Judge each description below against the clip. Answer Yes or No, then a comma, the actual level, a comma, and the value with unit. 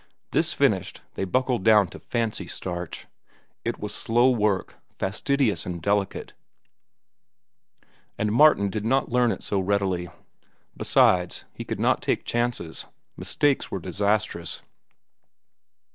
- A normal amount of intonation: Yes, average, 4.0 semitones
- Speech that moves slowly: Yes, slow, 120 wpm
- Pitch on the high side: No, low, 105 Hz